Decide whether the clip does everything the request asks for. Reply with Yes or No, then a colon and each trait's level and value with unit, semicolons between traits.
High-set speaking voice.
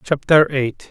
No: medium, 140 Hz